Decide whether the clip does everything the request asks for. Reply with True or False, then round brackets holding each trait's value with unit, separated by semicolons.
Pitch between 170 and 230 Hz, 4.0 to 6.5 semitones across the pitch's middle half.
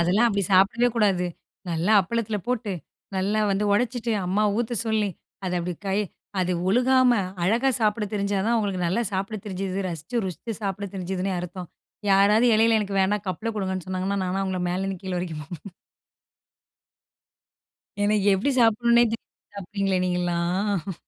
False (195 Hz; 3.0 semitones)